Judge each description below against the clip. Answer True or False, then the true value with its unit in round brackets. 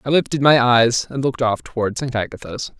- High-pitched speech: False (125 Hz)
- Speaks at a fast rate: True (215 wpm)